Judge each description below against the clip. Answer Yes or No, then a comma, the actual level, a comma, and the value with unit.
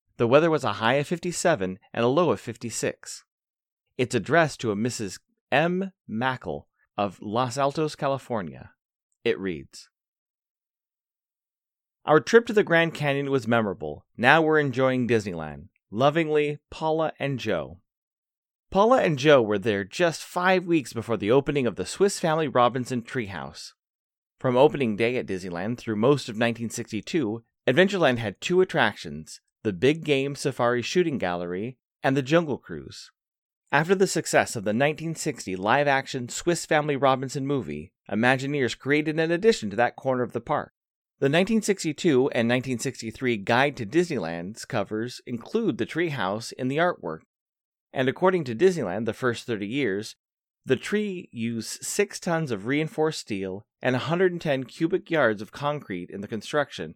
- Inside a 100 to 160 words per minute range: Yes, average, 150 wpm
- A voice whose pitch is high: No, low, 135 Hz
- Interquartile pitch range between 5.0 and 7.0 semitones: Yes, wide, 5.6 semitones